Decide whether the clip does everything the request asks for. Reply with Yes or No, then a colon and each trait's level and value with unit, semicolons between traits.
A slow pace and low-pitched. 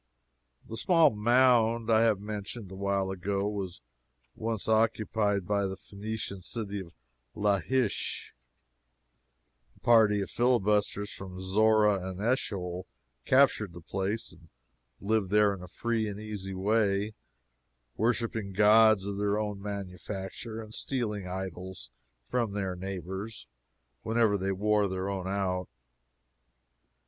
Yes: slow, 125 wpm; low, 105 Hz